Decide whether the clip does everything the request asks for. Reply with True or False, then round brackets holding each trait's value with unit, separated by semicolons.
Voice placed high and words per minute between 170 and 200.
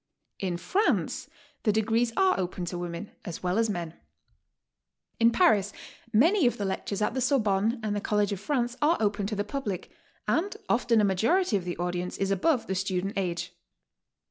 True (205 Hz; 185 wpm)